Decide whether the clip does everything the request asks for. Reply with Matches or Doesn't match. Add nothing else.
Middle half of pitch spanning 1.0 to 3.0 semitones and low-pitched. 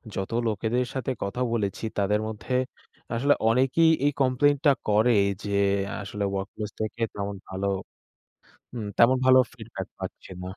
Doesn't match